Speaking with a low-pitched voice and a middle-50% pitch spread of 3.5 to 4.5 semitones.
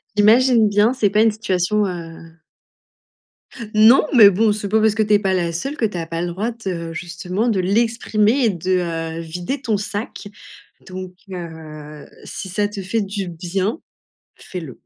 No: high, 195 Hz; average, 3.8 semitones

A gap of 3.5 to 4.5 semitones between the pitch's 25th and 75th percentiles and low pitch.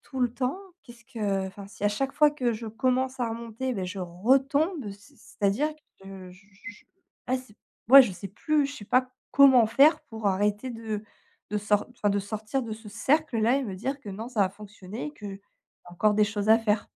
No: average, 4.1 semitones; high, 225 Hz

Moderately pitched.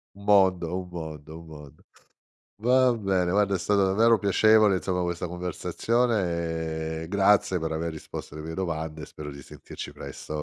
No: very low, 90 Hz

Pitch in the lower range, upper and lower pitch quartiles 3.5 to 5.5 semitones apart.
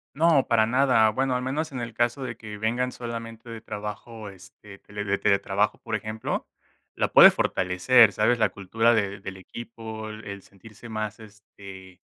No: low, 110 Hz; average, 2.7 semitones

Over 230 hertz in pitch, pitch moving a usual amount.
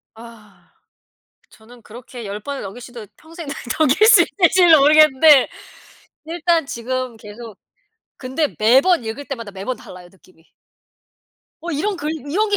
No: very high, 260 Hz; wide, 5.9 semitones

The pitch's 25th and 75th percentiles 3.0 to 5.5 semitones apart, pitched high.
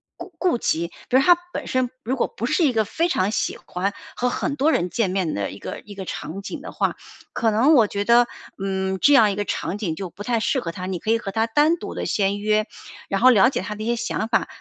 Yes: average, 4.4 semitones; high, 215 Hz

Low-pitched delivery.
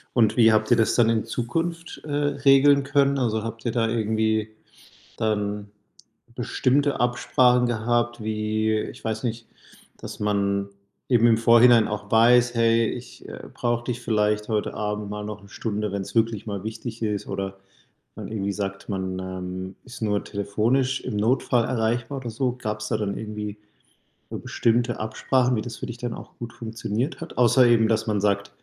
Yes: low, 110 Hz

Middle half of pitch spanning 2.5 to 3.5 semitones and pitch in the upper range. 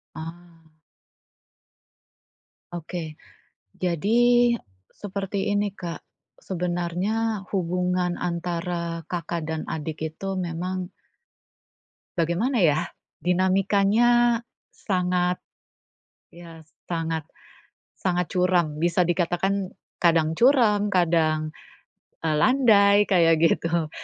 No: average, 3.0 semitones; medium, 180 Hz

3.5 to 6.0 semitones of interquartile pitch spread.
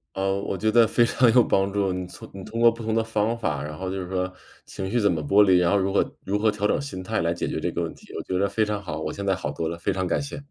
No: average, 3.1 semitones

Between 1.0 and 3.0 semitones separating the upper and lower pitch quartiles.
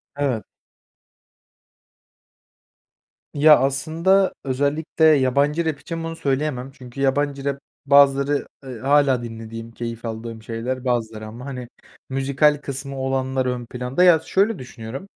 Yes: average, 2.7 semitones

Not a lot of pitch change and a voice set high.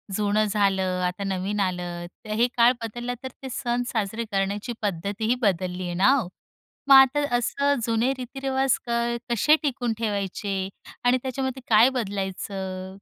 No: average, 4.2 semitones; high, 215 Hz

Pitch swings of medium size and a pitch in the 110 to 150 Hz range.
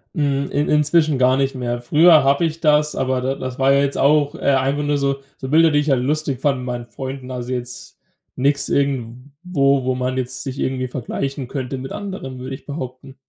No: narrow, 2.1 semitones; low, 135 Hz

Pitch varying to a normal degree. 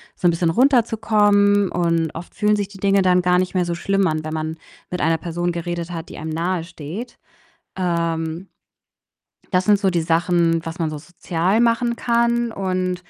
Yes: average, 3.5 semitones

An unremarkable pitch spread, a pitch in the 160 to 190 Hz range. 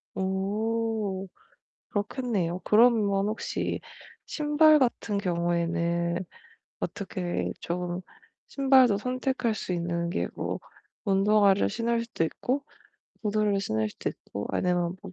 No: average, 4.7 semitones; high, 200 Hz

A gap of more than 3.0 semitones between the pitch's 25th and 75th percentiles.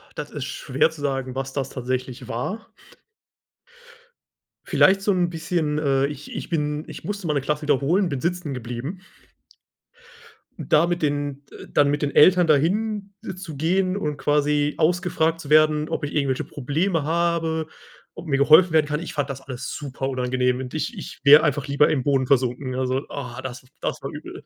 Yes: average, 3.5 semitones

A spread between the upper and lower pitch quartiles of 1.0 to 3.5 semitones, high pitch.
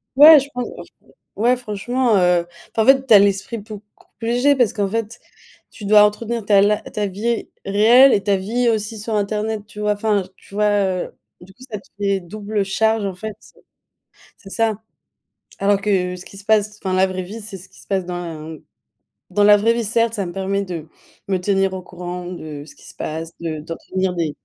Yes: average, 2.8 semitones; high, 205 Hz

